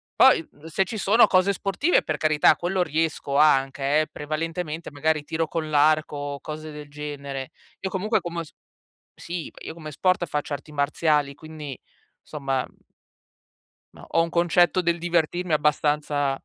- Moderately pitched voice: Yes, medium, 155 Hz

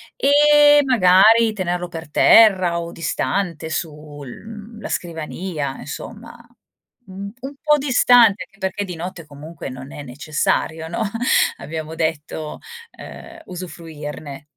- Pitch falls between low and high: Yes, medium, 175 Hz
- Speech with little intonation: No, wide, 5.9 semitones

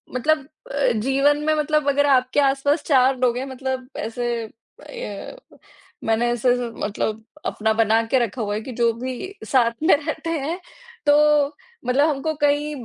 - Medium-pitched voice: No, very high, 270 Hz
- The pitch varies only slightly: No, average, 3.6 semitones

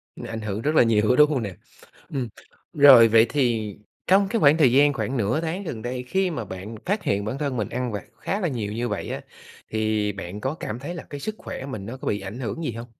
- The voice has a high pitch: No, low, 125 Hz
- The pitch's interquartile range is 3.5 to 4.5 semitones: No, average, 5.2 semitones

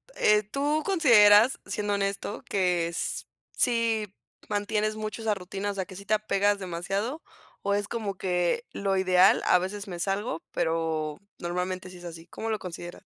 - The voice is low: No, high, 200 Hz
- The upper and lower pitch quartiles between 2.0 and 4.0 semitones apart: Yes, average, 2.9 semitones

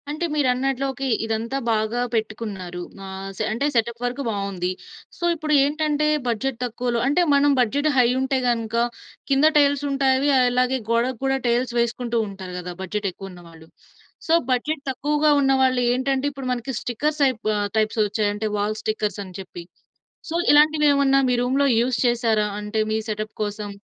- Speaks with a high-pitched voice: Yes, high, 245 Hz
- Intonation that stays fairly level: No, average, 4.1 semitones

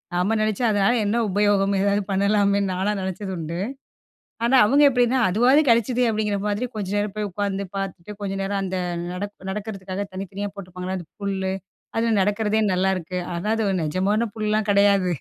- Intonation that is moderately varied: No, narrow, 1.9 semitones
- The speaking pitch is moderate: No, high, 200 Hz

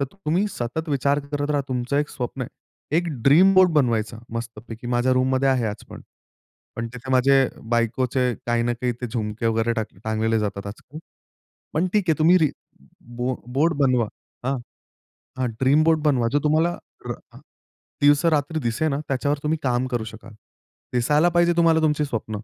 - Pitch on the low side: Yes, low, 130 Hz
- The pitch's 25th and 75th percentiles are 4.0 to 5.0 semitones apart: Yes, average, 4.3 semitones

